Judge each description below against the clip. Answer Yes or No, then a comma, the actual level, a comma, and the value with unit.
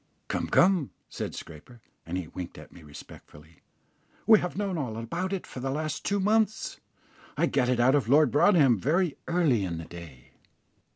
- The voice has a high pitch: No, low, 135 Hz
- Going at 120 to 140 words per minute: No, average, 180 wpm